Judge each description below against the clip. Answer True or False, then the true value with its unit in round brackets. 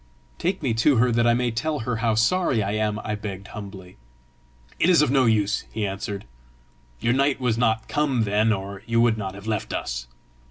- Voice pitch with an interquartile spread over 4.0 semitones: False (3.3 semitones)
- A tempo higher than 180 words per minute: True (205 wpm)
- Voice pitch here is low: True (110 Hz)